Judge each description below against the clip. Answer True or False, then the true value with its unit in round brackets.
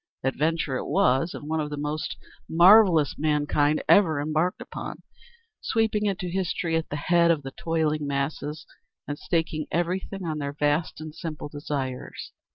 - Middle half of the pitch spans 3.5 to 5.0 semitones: False (2.7 semitones)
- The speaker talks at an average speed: True (155 wpm)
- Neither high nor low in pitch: True (155 Hz)